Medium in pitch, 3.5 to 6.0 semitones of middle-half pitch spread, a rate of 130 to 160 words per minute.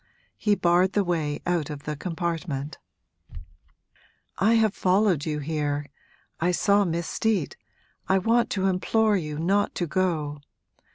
Yes: medium, 175 Hz; average, 4.6 semitones; slow, 135 wpm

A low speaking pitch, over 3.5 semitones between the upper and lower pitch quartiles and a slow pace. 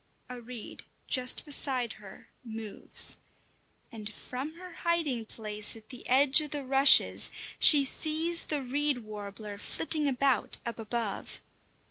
No: very high, 250 Hz; average, 4.7 semitones; slow, 130 wpm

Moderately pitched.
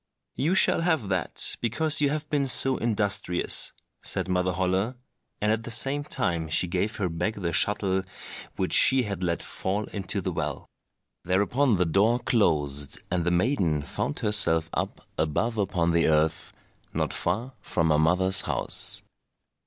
No: very low, 95 Hz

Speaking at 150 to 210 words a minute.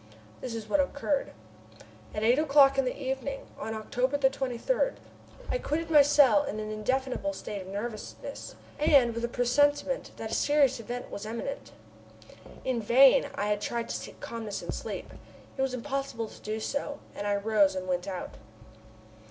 Yes: average, 170 wpm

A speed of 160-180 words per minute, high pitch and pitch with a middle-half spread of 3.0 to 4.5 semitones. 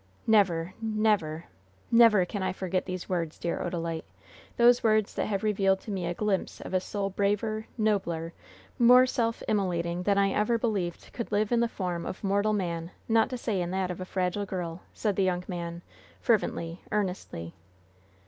Yes: average, 175 wpm; high, 195 Hz; average, 3.4 semitones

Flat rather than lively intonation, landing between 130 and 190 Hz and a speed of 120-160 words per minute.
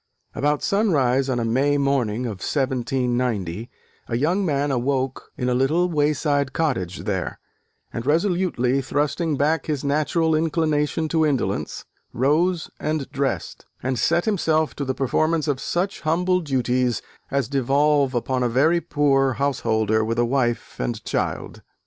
No: average, 3.8 semitones; medium, 140 Hz; average, 145 wpm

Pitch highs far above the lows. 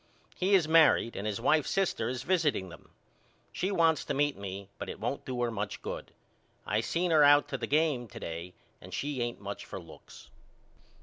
Yes: wide, 7.6 semitones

